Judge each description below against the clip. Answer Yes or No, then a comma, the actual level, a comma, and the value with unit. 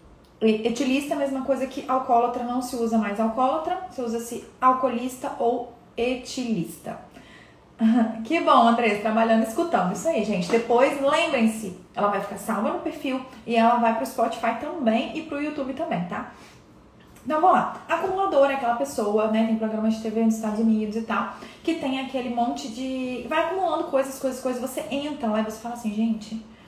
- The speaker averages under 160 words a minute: No, average, 180 wpm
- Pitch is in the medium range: No, high, 240 Hz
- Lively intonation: No, average, 3.6 semitones